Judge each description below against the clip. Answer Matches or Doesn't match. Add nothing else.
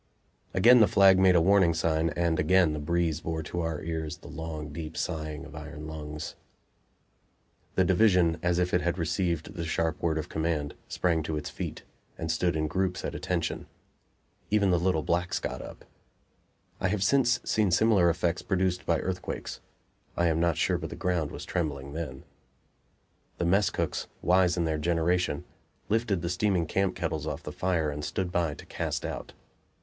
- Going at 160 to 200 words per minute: Matches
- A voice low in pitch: Matches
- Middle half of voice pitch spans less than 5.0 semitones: Matches